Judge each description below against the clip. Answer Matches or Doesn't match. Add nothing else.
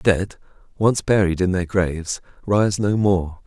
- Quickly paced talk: Doesn't match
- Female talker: Doesn't match